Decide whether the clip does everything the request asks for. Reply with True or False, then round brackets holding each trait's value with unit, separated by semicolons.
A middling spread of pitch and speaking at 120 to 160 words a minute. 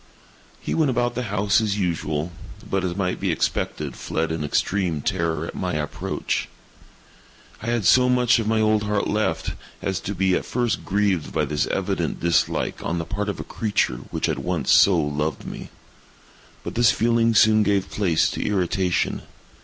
False (4.5 semitones; 175 wpm)